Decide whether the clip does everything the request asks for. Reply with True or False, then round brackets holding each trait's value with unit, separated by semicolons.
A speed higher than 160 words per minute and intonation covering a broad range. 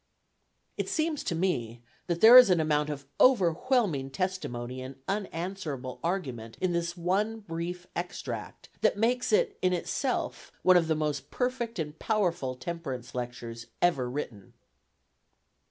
False (140 wpm; 6.6 semitones)